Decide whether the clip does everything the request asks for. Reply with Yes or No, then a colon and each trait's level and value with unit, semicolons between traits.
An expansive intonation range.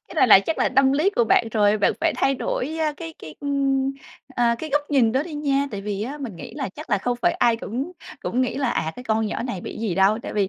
No: average, 4.9 semitones